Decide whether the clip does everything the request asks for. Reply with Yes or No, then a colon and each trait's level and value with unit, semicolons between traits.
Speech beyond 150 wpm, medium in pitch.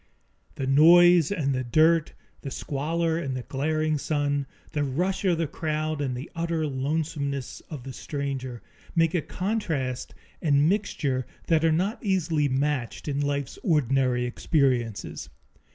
No: average, 140 wpm; medium, 150 Hz